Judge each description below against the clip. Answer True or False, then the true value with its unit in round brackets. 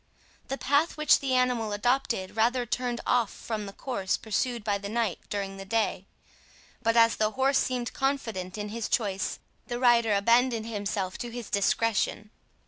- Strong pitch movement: False (3.3 semitones)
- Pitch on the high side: True (230 Hz)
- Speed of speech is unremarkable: True (165 wpm)